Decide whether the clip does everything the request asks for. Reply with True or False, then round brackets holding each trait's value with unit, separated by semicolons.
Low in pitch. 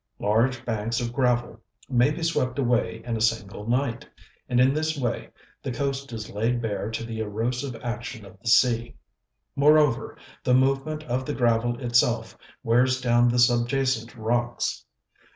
True (120 Hz)